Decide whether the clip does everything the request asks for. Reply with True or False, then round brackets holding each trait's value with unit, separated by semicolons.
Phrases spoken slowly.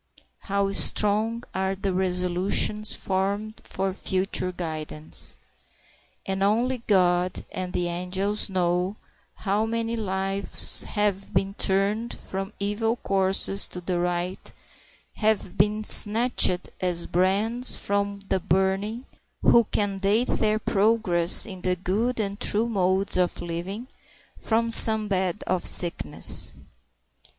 True (120 wpm)